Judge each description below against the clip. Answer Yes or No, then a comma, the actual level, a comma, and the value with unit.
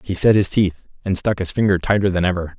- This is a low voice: Yes, very low, 95 Hz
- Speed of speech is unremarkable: No, fast, 255 wpm